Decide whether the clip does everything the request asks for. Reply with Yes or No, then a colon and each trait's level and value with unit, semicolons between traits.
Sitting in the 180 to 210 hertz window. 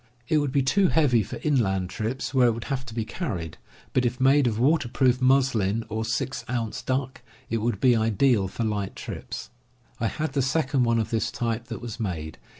No: low, 120 Hz